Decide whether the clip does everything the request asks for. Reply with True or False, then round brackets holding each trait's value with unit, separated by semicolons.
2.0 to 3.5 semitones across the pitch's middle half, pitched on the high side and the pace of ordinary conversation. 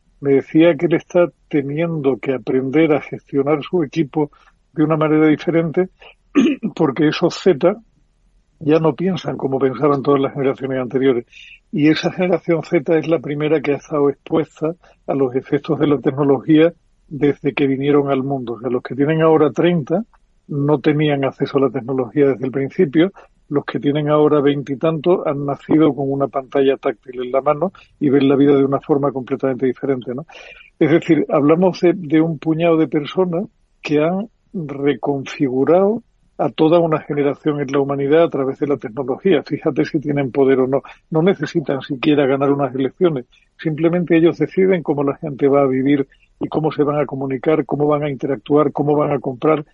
False (2.8 semitones; 150 Hz; 180 wpm)